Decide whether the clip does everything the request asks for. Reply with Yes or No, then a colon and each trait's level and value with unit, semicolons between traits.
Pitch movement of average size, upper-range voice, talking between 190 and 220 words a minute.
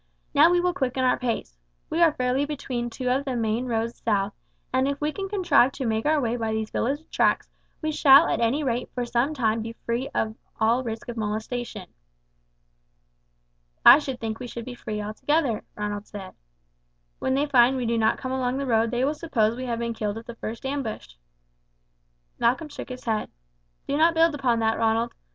Yes: average, 3.6 semitones; high, 245 Hz; average, 200 wpm